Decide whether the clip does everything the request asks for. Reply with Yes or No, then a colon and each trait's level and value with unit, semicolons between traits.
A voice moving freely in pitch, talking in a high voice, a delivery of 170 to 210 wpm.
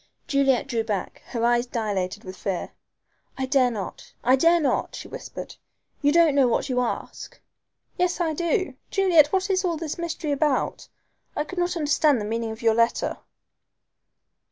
Yes: wide, 6.3 semitones; very high, 275 Hz; average, 175 wpm